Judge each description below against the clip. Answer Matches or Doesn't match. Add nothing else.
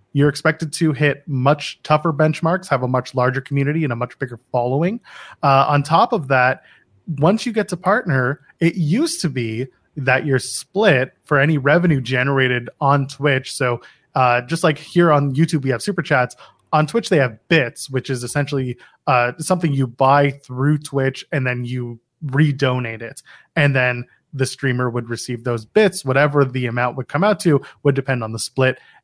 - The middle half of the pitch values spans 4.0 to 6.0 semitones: Doesn't match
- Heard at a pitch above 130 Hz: Matches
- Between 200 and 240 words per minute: Doesn't match